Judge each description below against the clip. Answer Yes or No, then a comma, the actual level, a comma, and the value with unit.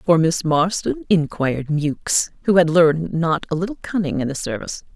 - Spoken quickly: No, average, 180 wpm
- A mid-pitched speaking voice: Yes, medium, 165 Hz